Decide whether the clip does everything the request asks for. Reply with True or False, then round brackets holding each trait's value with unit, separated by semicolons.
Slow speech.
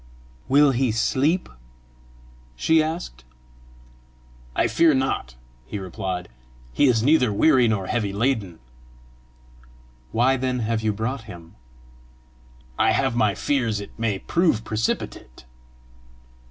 True (115 wpm)